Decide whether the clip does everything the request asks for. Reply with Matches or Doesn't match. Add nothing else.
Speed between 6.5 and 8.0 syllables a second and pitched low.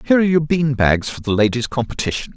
Matches